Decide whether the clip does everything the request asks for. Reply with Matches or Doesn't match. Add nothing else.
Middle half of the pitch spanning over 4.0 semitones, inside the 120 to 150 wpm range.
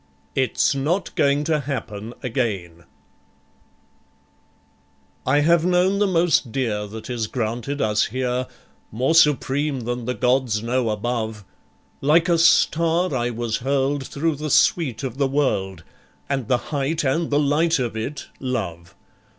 Matches